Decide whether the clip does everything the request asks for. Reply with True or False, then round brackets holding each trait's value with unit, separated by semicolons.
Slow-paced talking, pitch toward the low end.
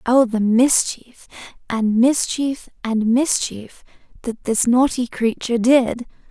False (115 wpm; 240 Hz)